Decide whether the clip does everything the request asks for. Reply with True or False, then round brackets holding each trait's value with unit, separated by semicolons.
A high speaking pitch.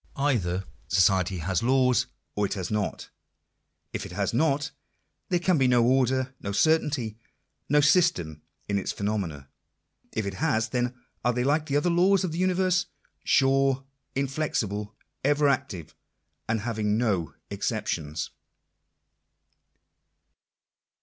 False (125 Hz)